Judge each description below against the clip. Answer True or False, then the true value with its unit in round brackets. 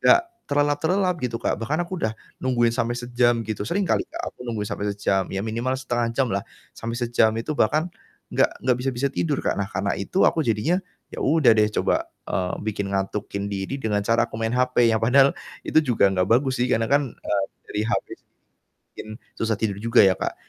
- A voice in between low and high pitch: False (120 Hz)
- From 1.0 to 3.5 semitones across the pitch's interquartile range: False (4.2 semitones)